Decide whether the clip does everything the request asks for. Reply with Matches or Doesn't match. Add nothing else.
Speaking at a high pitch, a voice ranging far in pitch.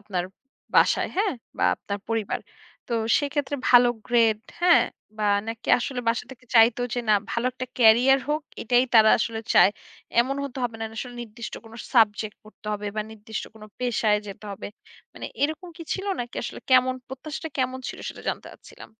Doesn't match